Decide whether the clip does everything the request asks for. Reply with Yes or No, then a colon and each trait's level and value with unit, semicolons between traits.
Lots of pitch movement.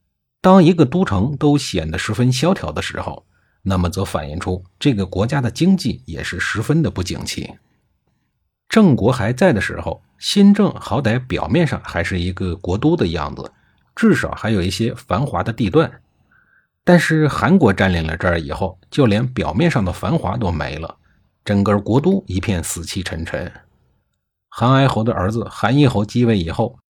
Yes: wide, 7.3 semitones